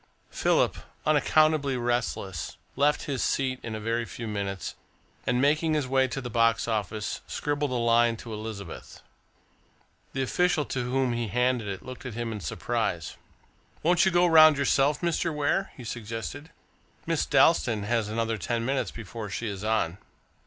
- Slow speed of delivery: No, average, 160 wpm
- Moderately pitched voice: No, low, 125 Hz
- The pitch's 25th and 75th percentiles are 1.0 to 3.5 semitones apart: No, average, 4.3 semitones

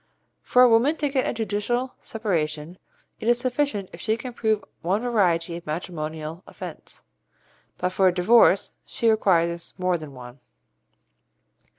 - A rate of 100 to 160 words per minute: Yes, average, 150 wpm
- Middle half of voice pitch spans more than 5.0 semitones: Yes, wide, 5.6 semitones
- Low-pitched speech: No, high, 195 Hz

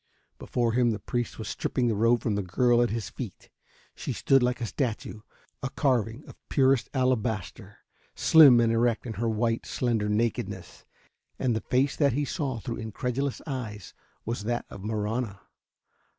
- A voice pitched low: Yes, low, 120 Hz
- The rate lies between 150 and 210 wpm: Yes, average, 165 wpm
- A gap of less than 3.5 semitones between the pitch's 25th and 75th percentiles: Yes, narrow, 2.4 semitones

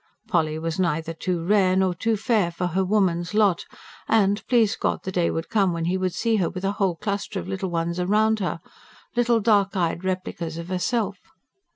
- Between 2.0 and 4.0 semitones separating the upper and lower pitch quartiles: Yes, average, 3.2 semitones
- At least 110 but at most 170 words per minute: No, average, 200 wpm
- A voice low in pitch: No, medium, 185 Hz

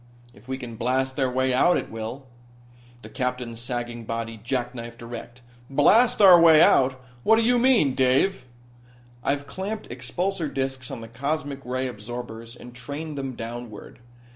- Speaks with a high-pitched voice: No, low, 130 Hz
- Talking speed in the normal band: Yes, average, 155 wpm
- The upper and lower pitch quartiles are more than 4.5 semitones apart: No, average, 3.2 semitones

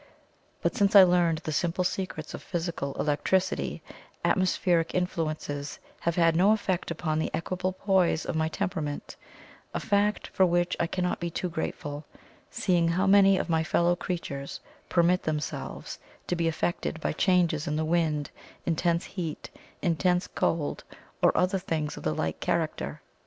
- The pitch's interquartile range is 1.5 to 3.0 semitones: Yes, narrow, 2.6 semitones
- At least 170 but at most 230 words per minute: No, average, 155 wpm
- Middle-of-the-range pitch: Yes, medium, 170 Hz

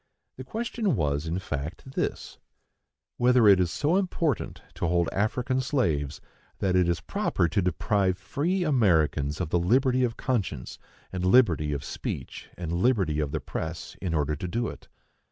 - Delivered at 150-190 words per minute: Yes, average, 160 wpm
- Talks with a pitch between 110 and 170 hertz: No, very low, 95 Hz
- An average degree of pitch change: No, wide, 7.8 semitones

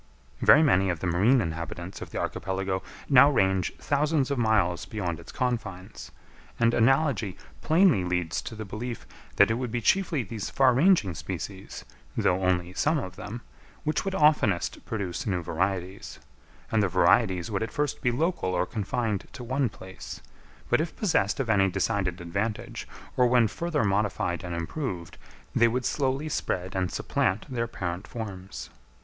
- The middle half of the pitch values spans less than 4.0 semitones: No, wide, 5.5 semitones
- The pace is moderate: Yes, average, 165 wpm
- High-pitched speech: No, low, 105 Hz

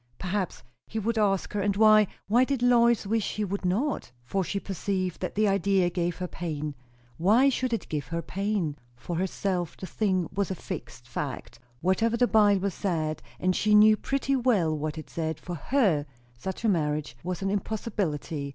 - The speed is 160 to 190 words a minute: Yes, average, 185 wpm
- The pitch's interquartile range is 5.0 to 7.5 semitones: No, average, 4.3 semitones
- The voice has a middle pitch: No, high, 195 Hz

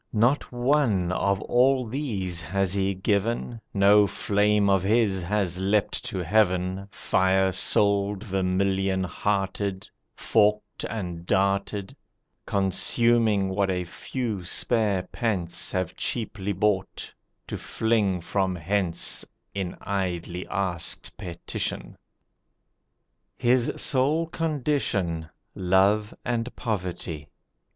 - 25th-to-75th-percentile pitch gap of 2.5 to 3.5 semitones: Yes, average, 2.8 semitones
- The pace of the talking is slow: Yes, slow, 95 wpm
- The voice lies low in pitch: Yes, low, 100 Hz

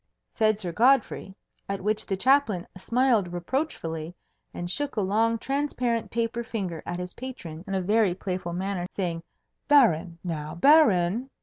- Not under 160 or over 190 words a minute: No, average, 145 wpm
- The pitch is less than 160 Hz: No, high, 200 Hz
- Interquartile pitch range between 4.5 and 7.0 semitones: Yes, average, 5.2 semitones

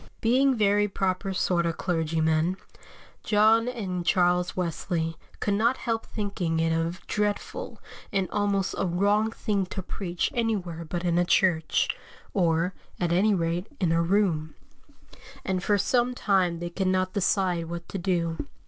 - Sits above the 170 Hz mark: Yes, medium, 185 Hz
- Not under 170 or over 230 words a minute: No, average, 150 wpm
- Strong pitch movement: No, average, 3.3 semitones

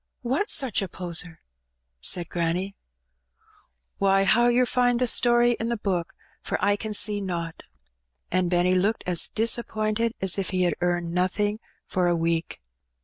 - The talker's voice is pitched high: Yes, high, 195 Hz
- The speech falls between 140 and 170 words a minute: Yes, average, 155 wpm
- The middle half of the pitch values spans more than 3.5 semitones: Yes, average, 4.3 semitones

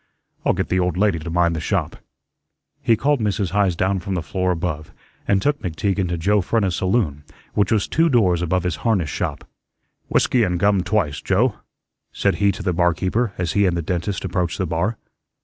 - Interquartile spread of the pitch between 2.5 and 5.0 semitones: Yes, average, 2.9 semitones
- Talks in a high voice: No, very low, 95 Hz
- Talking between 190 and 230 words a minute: Yes, average, 200 wpm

